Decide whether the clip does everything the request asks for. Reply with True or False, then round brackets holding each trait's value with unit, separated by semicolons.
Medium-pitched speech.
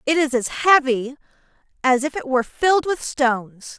False (275 Hz)